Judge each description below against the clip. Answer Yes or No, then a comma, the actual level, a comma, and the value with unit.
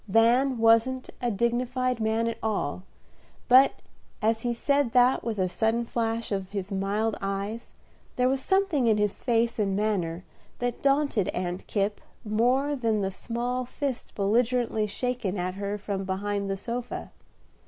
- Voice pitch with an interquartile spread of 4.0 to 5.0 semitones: No, average, 3.6 semitones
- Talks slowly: No, average, 155 wpm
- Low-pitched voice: No, high, 225 Hz